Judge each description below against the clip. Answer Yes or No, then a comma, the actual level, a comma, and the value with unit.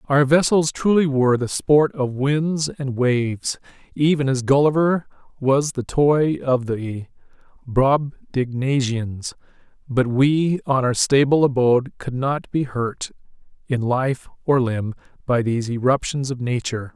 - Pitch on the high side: No, low, 135 Hz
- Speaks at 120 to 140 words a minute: Yes, slow, 135 wpm